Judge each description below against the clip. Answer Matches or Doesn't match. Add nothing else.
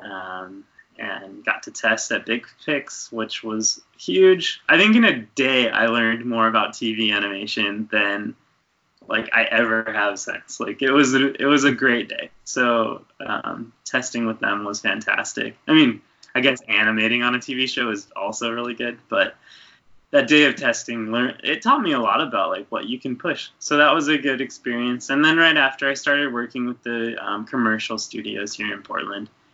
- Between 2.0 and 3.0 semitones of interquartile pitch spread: Doesn't match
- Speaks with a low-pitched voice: Matches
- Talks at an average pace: Matches